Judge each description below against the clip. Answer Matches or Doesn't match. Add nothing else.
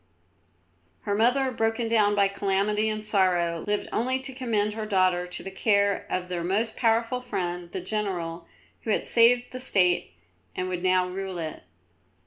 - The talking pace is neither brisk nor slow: Matches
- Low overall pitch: Doesn't match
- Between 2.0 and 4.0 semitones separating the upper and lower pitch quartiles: Matches